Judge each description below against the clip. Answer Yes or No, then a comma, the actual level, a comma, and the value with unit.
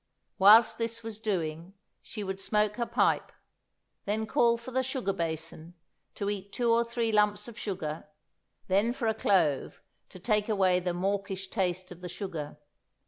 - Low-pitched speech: No, high, 200 Hz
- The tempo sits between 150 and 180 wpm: Yes, average, 165 wpm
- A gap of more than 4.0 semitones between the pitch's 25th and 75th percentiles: No, average, 3.6 semitones